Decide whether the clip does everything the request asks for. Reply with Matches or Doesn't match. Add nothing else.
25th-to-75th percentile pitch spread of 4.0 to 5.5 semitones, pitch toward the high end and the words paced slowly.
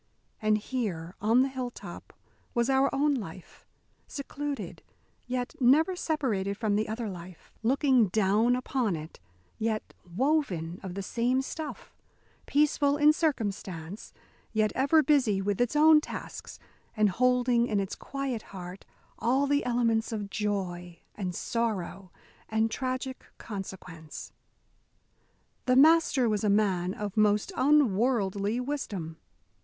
Matches